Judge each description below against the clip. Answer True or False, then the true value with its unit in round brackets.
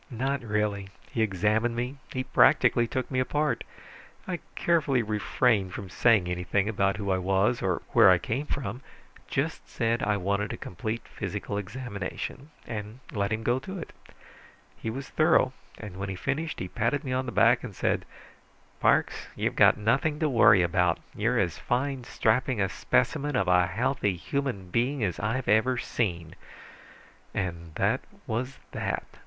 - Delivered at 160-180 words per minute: True (165 wpm)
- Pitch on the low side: True (115 Hz)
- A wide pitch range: False (4.8 semitones)